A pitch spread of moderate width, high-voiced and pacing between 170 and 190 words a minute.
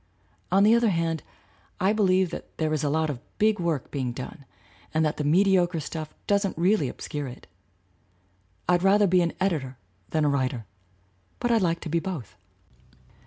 No: average, 4.5 semitones; medium, 165 Hz; average, 175 wpm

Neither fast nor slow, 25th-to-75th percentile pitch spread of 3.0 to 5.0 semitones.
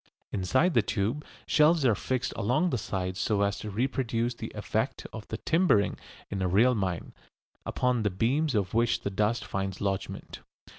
Yes: average, 170 wpm; average, 4.6 semitones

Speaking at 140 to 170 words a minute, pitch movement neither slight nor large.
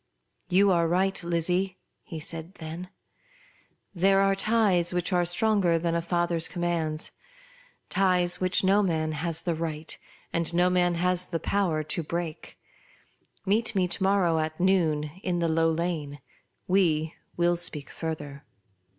No: average, 150 wpm; narrow, 2.2 semitones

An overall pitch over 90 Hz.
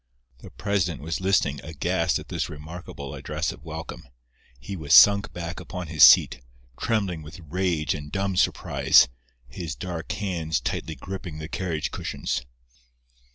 No: very low, 85 Hz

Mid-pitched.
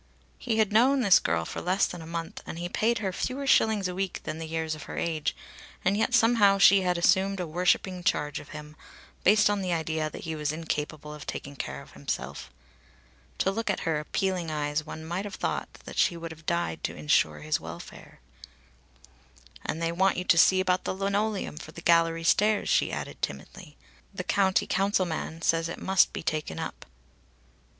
Yes: medium, 175 Hz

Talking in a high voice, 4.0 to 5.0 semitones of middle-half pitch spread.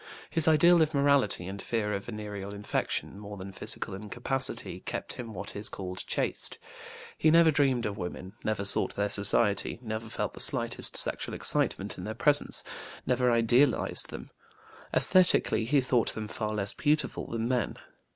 No: low, 110 Hz; average, 4.7 semitones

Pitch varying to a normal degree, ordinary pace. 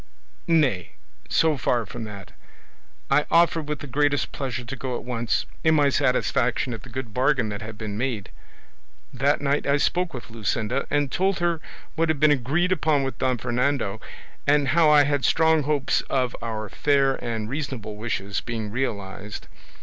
Yes: average, 4.3 semitones; average, 175 wpm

